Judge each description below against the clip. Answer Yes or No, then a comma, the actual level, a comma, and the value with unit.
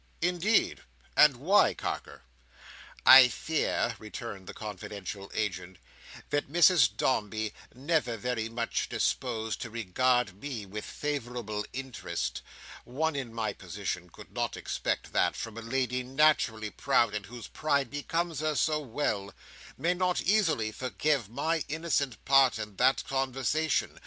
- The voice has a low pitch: Yes, low, 125 Hz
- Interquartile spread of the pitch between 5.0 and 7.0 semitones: Yes, wide, 5.4 semitones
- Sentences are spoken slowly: Yes, slow, 125 wpm